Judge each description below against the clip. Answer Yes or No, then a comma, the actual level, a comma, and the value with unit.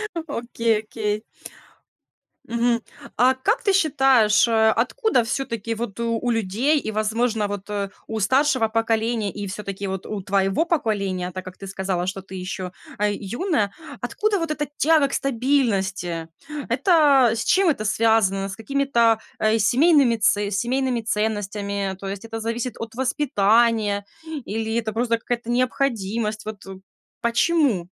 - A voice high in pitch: Yes, high, 225 Hz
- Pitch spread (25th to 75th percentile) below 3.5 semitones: No, average, 3.9 semitones